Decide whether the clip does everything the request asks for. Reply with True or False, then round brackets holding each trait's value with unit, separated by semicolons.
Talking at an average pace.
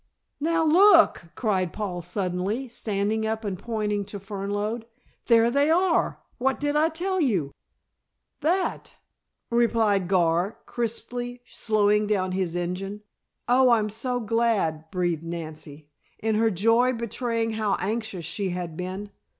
False (130 wpm)